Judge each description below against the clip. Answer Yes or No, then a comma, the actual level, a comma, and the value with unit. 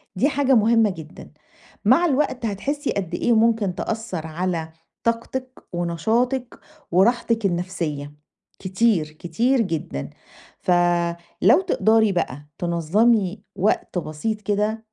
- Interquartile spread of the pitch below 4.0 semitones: No, average, 5.1 semitones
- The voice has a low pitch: No, high, 210 Hz